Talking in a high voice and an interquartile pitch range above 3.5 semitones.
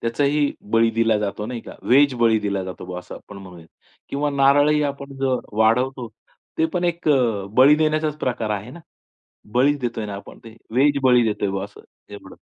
No: low, 125 Hz; average, 5.1 semitones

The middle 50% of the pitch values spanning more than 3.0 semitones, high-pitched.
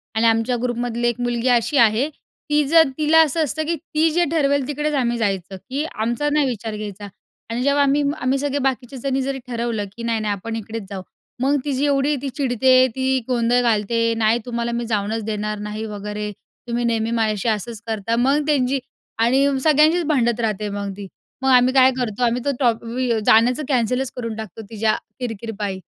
Yes: average, 3.5 semitones; high, 240 Hz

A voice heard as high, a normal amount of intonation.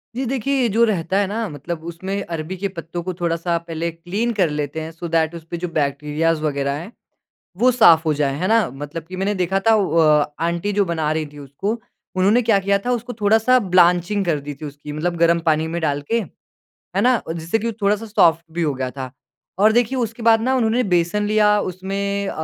No: medium, 175 Hz; average, 4.6 semitones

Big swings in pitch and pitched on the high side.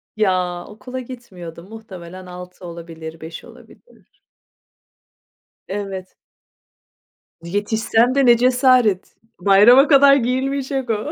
Yes: wide, 5.9 semitones; high, 210 Hz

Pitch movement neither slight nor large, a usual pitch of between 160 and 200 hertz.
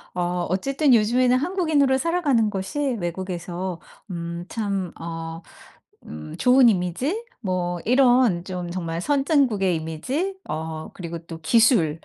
No: wide, 7.3 semitones; high, 190 Hz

